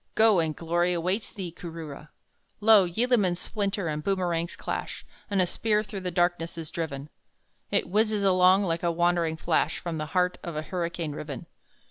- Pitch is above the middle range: No, medium, 175 Hz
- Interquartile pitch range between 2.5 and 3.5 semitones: Yes, average, 2.9 semitones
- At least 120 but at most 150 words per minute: No, average, 170 wpm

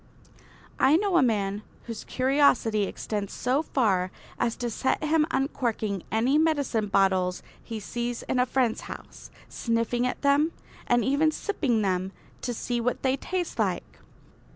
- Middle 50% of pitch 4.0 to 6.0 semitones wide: Yes, average, 4.6 semitones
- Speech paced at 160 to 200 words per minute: No, average, 150 wpm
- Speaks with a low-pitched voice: No, high, 240 Hz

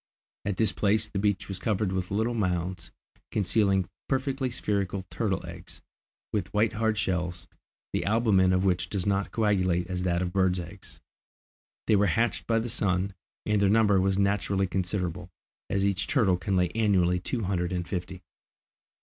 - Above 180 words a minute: No, average, 165 wpm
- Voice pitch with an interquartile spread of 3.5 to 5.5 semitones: No, narrow, 2.6 semitones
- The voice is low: Yes, very low, 95 Hz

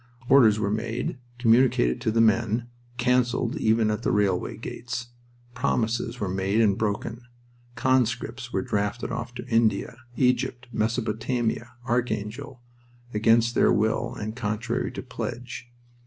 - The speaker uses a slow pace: Yes, slow, 125 wpm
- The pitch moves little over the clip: Yes, narrow, 2.2 semitones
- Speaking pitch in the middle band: No, low, 115 Hz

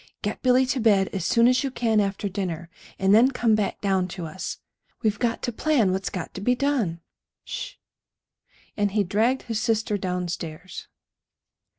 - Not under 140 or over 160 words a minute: No, average, 180 wpm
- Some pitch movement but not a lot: Yes, average, 4.3 semitones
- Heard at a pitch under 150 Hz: No, high, 210 Hz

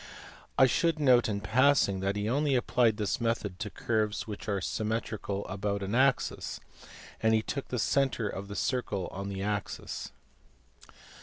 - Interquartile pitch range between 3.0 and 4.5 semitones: Yes, average, 3.6 semitones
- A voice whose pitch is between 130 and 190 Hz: No, low, 110 Hz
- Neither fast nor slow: Yes, average, 160 wpm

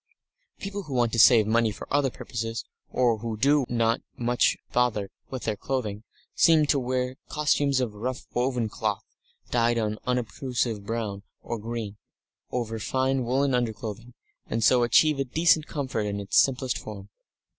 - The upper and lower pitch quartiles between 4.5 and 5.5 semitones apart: No, average, 2.9 semitones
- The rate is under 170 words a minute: Yes, average, 160 wpm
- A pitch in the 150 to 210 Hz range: No, low, 120 Hz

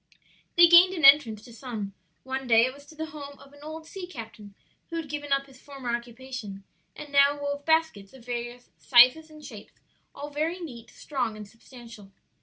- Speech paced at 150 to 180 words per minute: No, average, 195 wpm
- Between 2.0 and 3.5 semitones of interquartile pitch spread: No, average, 4.2 semitones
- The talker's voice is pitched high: Yes, very high, 275 Hz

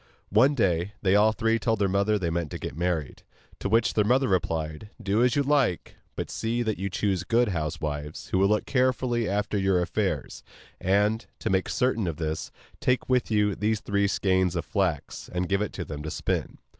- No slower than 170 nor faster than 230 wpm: Yes, fast, 205 wpm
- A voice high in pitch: No, low, 100 Hz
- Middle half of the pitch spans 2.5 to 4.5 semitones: Yes, average, 4.2 semitones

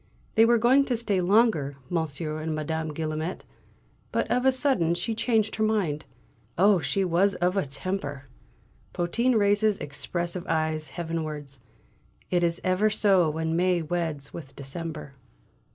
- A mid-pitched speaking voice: Yes, medium, 175 Hz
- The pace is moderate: Yes, average, 145 wpm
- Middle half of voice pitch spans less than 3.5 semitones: No, average, 4.7 semitones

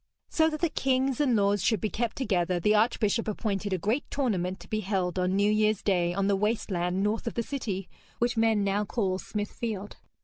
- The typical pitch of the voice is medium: No, high, 210 Hz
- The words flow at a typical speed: No, fast, 210 wpm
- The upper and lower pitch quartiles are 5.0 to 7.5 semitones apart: No, average, 3.2 semitones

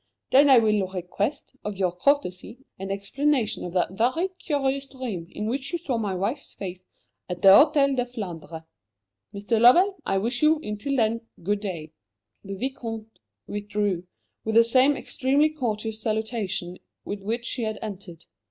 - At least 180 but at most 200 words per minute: No, average, 160 wpm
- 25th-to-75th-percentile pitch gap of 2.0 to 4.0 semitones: No, average, 5.3 semitones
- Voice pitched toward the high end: Yes, high, 220 Hz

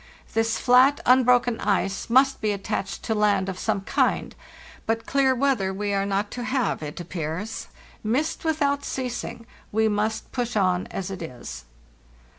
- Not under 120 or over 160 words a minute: Yes, average, 155 wpm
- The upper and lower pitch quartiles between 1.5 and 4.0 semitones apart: No, average, 4.4 semitones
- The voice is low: No, high, 220 Hz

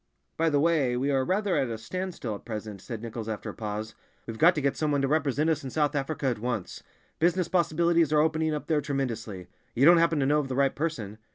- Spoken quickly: Yes, fast, 240 wpm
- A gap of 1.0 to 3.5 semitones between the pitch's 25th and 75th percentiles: No, wide, 5.4 semitones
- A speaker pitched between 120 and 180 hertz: Yes, medium, 140 Hz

